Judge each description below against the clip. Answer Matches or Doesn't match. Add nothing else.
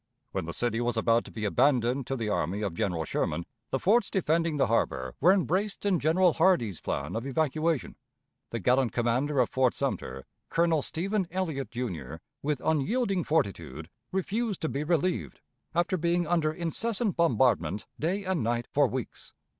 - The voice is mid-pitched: Matches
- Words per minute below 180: Matches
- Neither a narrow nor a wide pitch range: Doesn't match